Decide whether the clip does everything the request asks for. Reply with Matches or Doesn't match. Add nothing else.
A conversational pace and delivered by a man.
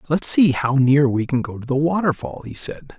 Doesn't match